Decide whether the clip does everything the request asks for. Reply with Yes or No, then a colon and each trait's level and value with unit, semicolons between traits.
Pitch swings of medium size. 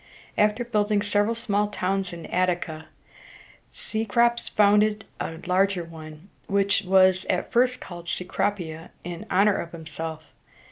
Yes: average, 3.4 semitones